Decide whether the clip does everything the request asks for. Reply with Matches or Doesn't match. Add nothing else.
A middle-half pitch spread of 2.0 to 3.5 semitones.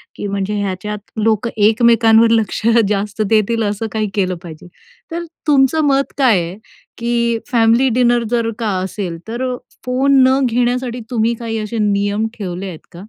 Matches